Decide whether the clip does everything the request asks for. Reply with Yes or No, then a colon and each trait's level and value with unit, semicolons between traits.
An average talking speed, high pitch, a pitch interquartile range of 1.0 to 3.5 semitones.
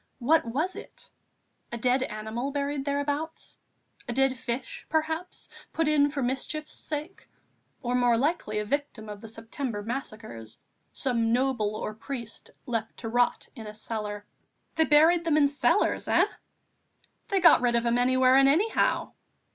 No: average, 155 wpm; very high, 255 Hz; average, 4.3 semitones